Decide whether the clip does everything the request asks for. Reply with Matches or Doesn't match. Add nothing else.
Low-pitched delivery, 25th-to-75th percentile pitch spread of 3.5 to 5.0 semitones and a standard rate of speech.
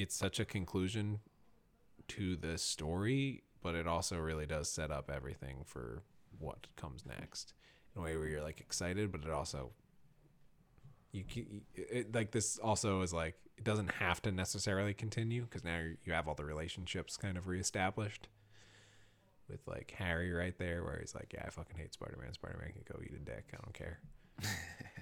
Matches